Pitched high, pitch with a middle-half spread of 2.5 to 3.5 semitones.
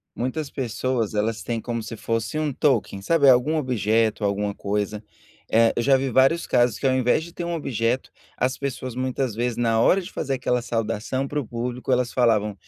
No: low, 125 Hz; average, 2.9 semitones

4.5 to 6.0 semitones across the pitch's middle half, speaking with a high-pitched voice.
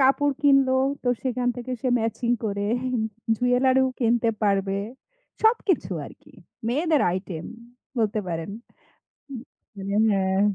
Yes: average, 4.9 semitones; high, 240 Hz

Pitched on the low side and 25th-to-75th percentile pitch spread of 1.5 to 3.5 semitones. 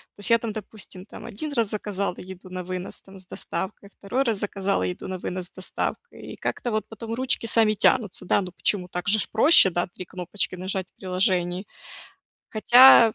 No: high, 195 Hz; average, 3.1 semitones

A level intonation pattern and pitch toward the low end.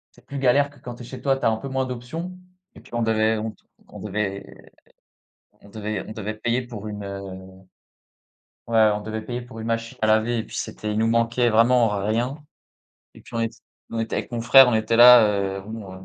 Yes: narrow, 2.2 semitones; low, 115 Hz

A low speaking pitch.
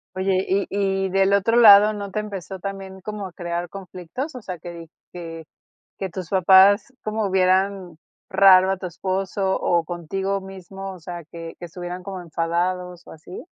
No: high, 190 Hz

